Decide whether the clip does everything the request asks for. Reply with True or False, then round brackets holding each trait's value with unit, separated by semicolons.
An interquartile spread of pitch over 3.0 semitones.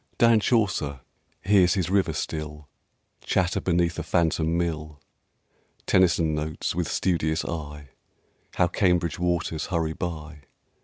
False (2.6 semitones)